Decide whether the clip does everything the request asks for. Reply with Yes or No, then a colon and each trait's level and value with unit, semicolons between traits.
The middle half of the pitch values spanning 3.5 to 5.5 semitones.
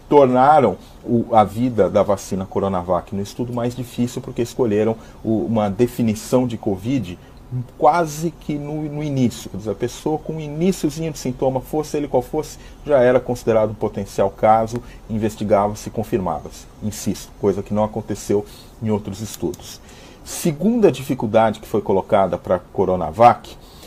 Yes: average, 4.0 semitones